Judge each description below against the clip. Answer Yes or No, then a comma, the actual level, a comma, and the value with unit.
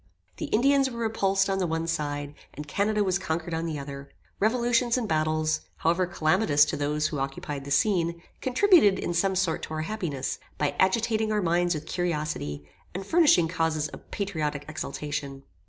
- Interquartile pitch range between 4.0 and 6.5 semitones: Yes, wide, 5.4 semitones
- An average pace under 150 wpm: No, average, 170 wpm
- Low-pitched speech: No, medium, 170 Hz